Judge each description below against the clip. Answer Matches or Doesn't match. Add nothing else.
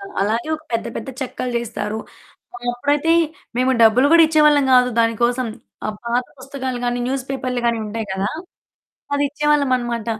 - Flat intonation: Doesn't match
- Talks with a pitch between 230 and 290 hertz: Matches